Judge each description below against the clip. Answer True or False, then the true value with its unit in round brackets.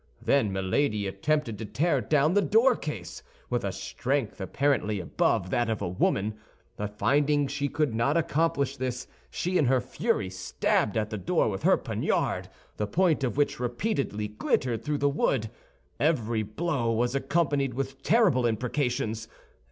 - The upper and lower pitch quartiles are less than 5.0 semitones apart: False (5.3 semitones)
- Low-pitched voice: True (130 Hz)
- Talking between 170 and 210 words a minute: False (155 wpm)